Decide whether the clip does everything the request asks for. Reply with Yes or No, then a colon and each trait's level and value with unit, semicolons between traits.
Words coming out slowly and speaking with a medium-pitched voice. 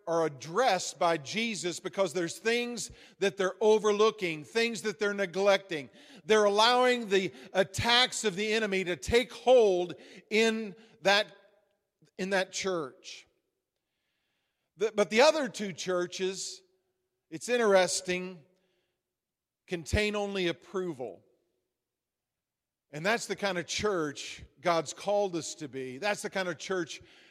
No: slow, 120 wpm; high, 195 Hz